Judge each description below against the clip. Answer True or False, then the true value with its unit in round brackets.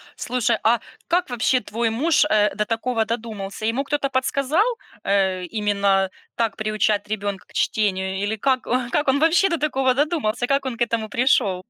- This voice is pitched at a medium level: False (230 Hz)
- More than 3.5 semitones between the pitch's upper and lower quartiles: True (4.3 semitones)